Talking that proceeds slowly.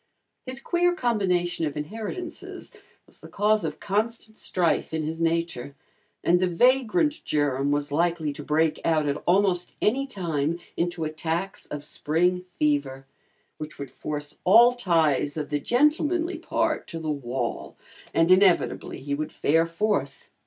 No: average, 145 wpm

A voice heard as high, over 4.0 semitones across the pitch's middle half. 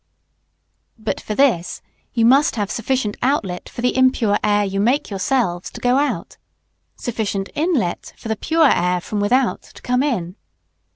Yes: high, 225 Hz; average, 4.6 semitones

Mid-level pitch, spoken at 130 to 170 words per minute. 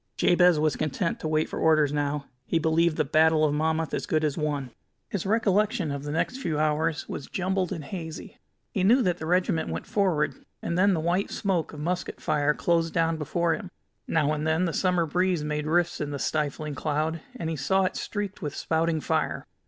No: medium, 160 Hz; fast, 205 wpm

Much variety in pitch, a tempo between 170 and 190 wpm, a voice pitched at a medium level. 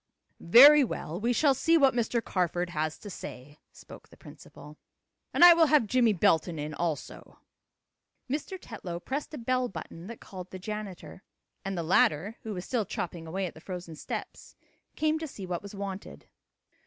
No: wide, 6.5 semitones; average, 180 wpm; high, 195 Hz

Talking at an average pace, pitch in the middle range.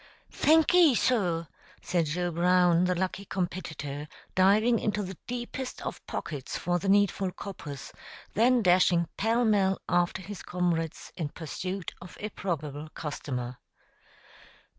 No: slow, 125 wpm; medium, 180 Hz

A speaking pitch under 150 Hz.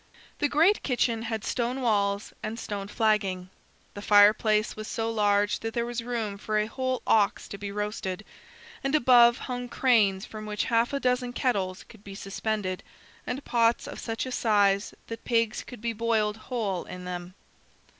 No: high, 220 Hz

